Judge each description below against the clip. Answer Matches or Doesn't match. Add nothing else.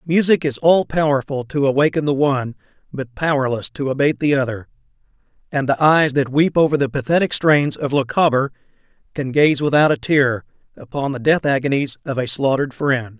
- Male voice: Matches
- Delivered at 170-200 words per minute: Matches